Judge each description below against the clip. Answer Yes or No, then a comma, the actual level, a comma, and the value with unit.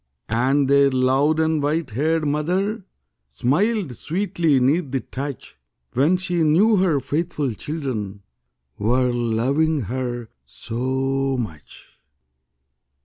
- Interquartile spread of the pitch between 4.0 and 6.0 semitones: Yes, average, 4.3 semitones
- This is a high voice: No, medium, 140 Hz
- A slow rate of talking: Yes, slow, 105 wpm